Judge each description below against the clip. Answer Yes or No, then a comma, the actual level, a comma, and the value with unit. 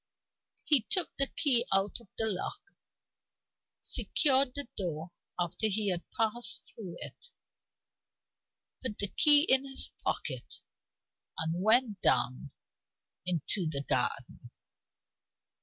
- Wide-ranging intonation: Yes, wide, 6.9 semitones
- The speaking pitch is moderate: No, high, 215 Hz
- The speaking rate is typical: No, slow, 110 wpm